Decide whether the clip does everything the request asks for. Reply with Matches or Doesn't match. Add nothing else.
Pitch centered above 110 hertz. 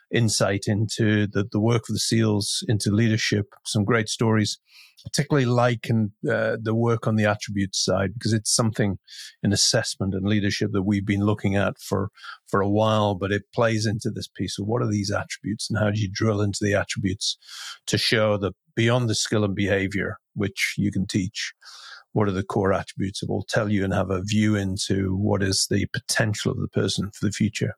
Doesn't match